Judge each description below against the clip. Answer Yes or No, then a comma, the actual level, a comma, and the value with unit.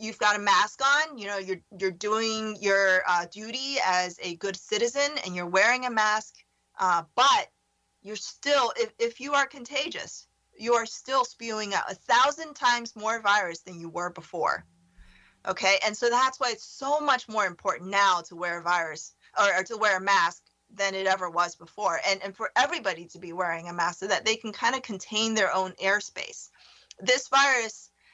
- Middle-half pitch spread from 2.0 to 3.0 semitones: No, average, 4.9 semitones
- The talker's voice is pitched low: No, high, 210 Hz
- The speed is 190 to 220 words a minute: Yes, average, 195 wpm